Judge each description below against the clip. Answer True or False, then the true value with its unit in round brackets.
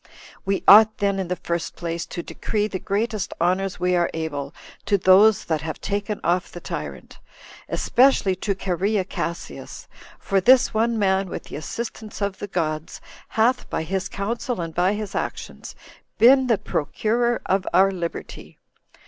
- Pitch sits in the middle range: False (195 Hz)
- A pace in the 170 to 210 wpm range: False (160 wpm)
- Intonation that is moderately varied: True (3.5 semitones)